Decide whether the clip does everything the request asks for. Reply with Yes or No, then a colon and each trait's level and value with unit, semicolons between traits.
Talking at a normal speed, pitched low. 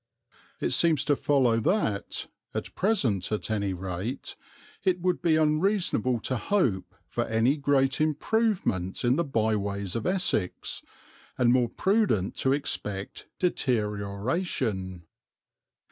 No: slow, 115 wpm; low, 125 Hz